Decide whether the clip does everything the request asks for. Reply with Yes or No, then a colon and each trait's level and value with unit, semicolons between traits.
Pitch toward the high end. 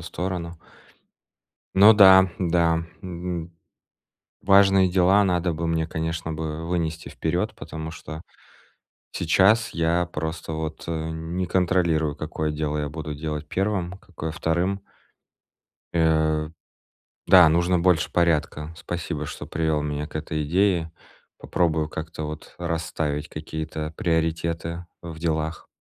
No: very low, 80 Hz